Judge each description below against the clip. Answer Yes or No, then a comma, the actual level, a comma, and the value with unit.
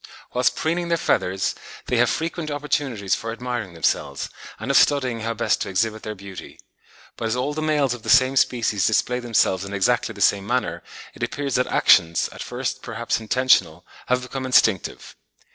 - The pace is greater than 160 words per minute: Yes, average, 180 wpm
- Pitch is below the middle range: Yes, low, 120 Hz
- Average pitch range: Yes, average, 4.5 semitones